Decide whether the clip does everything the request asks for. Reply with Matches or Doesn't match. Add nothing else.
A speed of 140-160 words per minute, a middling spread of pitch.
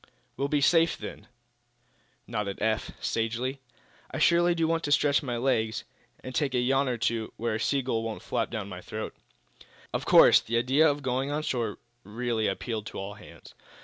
Doesn't match